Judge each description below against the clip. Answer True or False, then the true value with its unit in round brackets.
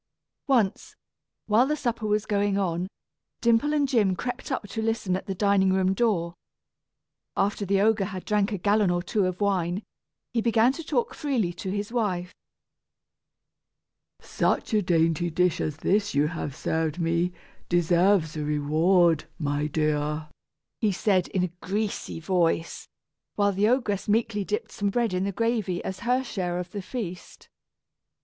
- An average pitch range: True (3.8 semitones)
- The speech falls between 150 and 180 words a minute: True (160 wpm)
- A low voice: False (195 Hz)